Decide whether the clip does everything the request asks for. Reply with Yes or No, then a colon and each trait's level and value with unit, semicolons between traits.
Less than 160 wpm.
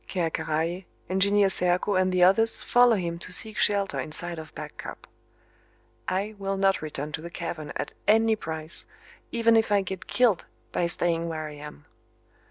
No: average, 175 wpm